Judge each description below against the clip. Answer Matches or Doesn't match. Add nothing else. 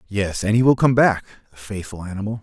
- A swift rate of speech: Matches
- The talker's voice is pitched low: Matches